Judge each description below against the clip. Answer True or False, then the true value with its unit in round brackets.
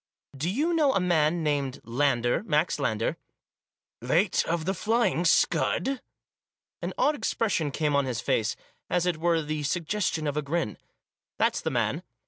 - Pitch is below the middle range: False (160 Hz)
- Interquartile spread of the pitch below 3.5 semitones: False (4.2 semitones)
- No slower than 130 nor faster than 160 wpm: False (175 wpm)